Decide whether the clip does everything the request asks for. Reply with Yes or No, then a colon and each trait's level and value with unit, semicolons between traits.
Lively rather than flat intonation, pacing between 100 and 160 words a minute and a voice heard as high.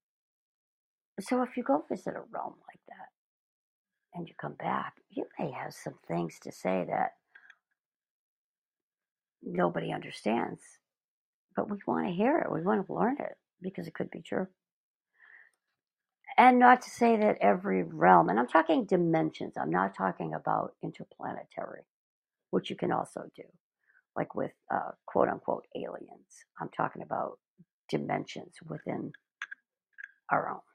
Yes: wide, 7.7 semitones; average, 140 wpm; high, 195 Hz